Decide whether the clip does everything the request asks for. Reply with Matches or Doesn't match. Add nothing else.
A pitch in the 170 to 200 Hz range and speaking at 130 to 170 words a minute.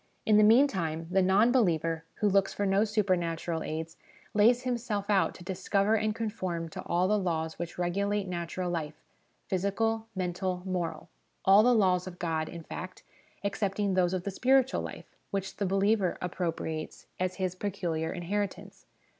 Matches